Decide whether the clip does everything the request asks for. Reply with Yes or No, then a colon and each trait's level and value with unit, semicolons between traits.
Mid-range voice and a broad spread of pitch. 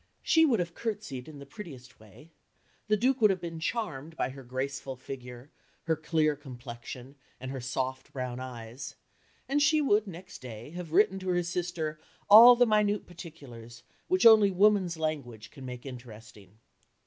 Yes: medium, 155 Hz; wide, 7.2 semitones